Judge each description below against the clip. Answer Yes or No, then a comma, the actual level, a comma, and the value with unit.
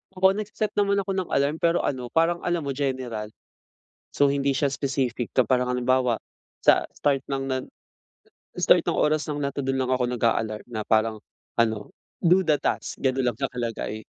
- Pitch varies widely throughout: No, average, 3.5 semitones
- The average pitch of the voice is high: No, low, 135 Hz